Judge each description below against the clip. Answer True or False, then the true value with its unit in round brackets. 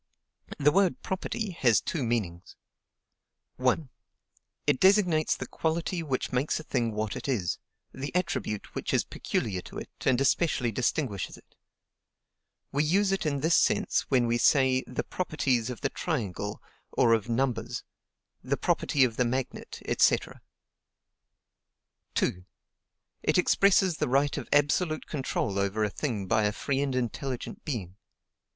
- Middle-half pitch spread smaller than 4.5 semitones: False (5.4 semitones)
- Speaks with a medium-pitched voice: False (130 Hz)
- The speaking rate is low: False (145 wpm)